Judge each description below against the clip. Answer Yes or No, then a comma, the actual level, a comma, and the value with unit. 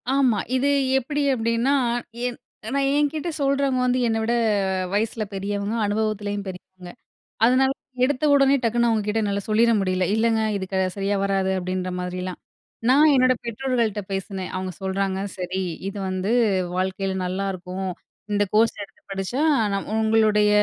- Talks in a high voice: Yes, high, 210 Hz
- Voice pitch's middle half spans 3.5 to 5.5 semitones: Yes, average, 4.2 semitones